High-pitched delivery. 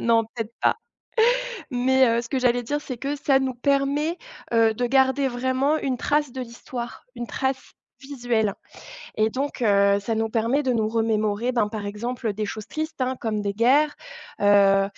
Yes: high, 240 Hz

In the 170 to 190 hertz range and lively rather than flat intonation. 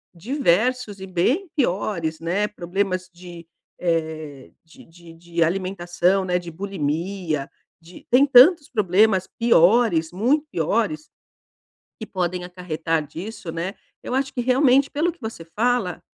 Yes: medium, 185 Hz; wide, 5.8 semitones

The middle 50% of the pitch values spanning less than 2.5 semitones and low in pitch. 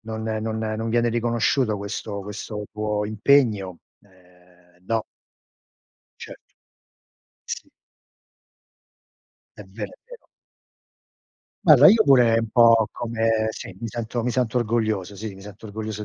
Yes: narrow, 2.1 semitones; low, 110 Hz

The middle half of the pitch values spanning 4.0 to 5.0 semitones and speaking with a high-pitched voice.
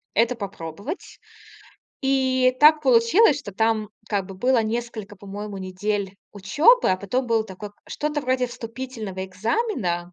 Yes: average, 4.7 semitones; high, 225 Hz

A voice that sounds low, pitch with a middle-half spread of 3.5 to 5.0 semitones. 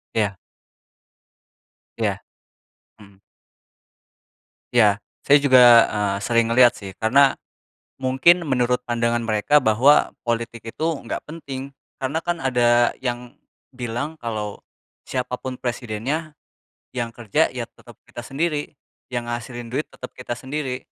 No: low, 125 Hz; narrow, 2.6 semitones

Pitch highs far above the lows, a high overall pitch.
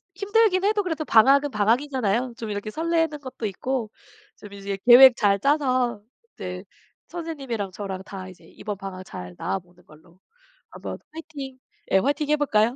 Yes: wide, 6.7 semitones; high, 240 Hz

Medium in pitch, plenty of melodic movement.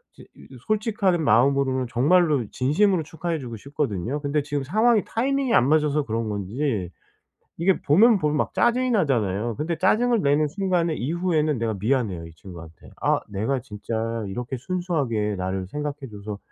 Yes: medium, 145 Hz; wide, 7.4 semitones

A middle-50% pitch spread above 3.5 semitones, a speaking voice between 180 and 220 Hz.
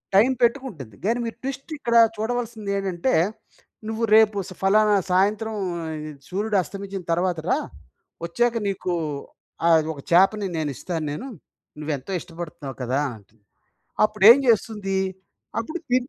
Yes: average, 4.9 semitones; high, 200 Hz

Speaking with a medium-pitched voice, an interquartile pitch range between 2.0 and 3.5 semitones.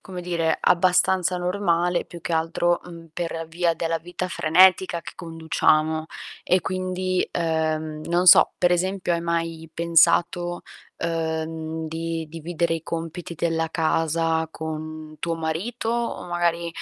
No: medium, 165 Hz; narrow, 1.6 semitones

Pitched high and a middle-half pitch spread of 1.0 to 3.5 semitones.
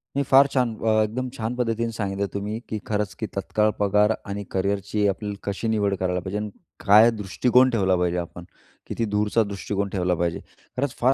No: low, 105 Hz; narrow, 2.5 semitones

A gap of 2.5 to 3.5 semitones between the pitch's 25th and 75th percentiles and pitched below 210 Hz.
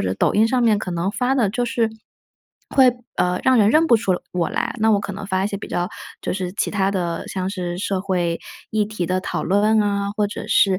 Yes: average, 2.8 semitones; high, 200 Hz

